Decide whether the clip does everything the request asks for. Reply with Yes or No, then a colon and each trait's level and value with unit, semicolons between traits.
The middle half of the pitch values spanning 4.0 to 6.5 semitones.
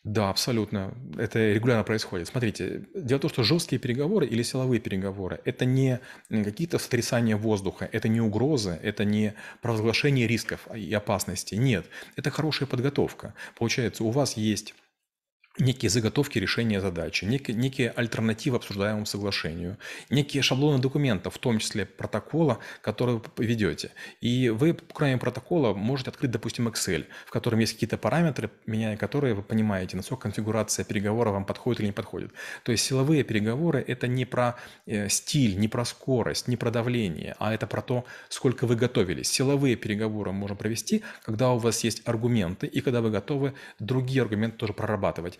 No: average, 3.4 semitones